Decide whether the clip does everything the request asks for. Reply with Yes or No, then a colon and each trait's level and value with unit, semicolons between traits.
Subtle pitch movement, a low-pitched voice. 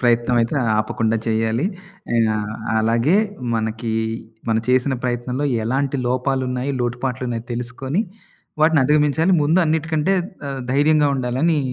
No: average, 3.9 semitones; low, 125 Hz